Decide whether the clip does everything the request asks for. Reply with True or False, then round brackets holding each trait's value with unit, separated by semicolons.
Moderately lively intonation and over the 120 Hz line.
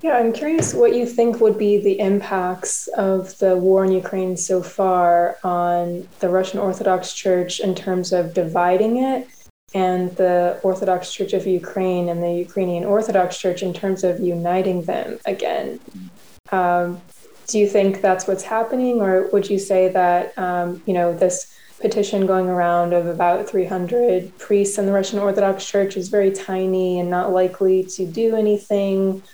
False (1.8 semitones; 190 Hz)